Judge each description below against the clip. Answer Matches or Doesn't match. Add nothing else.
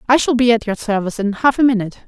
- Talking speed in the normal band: Doesn't match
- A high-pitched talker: Matches